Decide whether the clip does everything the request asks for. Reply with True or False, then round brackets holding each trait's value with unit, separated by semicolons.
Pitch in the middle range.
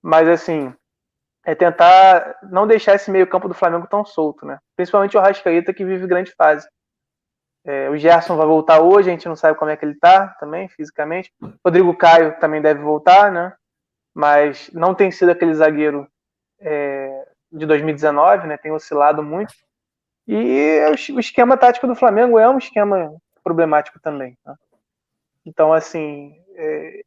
True (170 Hz)